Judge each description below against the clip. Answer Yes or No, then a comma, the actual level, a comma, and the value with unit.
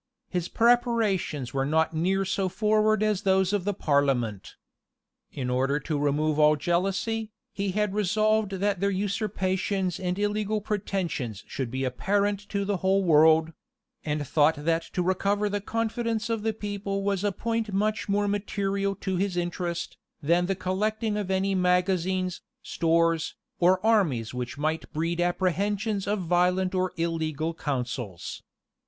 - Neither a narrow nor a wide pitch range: Yes, average, 4.0 semitones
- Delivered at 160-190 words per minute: No, average, 150 wpm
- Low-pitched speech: No, high, 190 Hz